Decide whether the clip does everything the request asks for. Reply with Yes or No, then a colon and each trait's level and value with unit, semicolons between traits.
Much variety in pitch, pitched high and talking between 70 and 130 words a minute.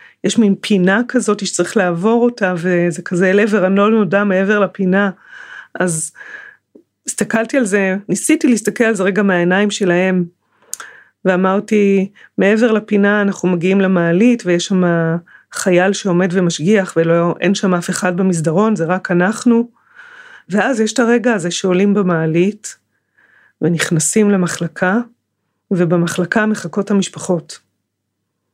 No: average, 3.3 semitones; high, 195 Hz; average, 120 wpm